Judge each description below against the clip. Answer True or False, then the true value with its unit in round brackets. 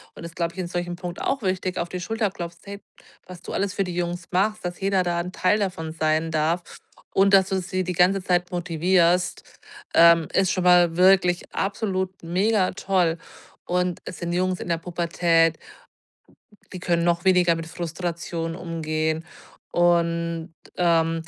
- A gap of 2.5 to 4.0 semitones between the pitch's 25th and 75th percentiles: False (1.8 semitones)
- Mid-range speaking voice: True (175 Hz)